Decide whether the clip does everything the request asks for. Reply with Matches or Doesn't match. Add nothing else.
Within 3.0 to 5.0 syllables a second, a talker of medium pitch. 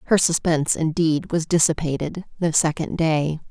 Matches